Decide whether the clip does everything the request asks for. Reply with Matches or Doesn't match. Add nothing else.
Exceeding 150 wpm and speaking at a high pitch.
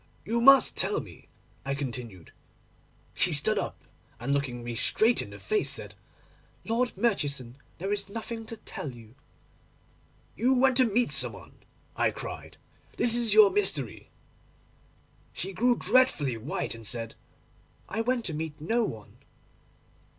Doesn't match